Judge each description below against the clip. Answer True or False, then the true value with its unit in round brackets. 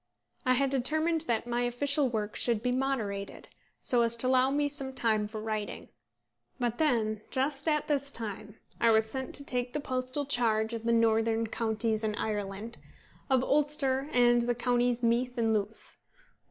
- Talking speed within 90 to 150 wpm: False (170 wpm)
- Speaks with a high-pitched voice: True (240 Hz)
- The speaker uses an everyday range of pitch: True (3.2 semitones)